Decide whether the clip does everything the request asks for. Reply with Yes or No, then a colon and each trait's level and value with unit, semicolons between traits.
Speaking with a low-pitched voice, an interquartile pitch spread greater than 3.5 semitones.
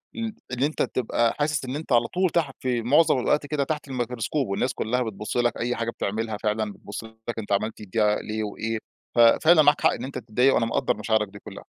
Yes: low, 120 Hz; average, 4.1 semitones